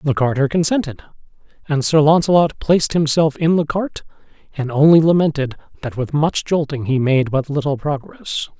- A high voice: No, medium, 150 Hz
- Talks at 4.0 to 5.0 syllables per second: No, 5.2 syllables/s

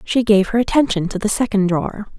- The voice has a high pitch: Yes, high, 210 Hz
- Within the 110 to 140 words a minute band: No, fast, 220 wpm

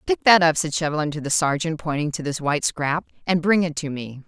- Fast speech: Yes, fast, 255 wpm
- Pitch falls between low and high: Yes, medium, 155 Hz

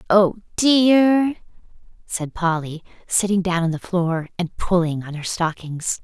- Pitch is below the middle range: No, medium, 185 Hz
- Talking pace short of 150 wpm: Yes, average, 140 wpm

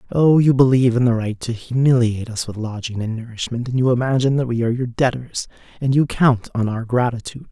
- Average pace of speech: No, fast, 215 wpm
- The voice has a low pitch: Yes, low, 120 Hz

